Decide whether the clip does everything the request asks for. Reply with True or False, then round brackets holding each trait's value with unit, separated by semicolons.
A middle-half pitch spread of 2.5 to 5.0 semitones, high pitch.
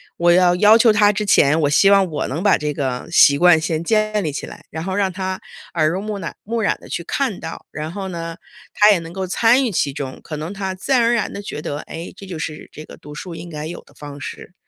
False (4.7 semitones; 175 Hz)